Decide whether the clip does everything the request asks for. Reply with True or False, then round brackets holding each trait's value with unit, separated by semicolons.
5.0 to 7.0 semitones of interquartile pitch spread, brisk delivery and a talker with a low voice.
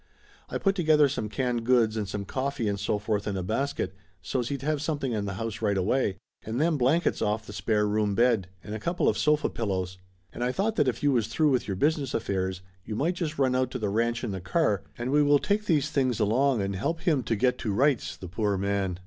True (5.5 semitones; 250 wpm; 120 Hz)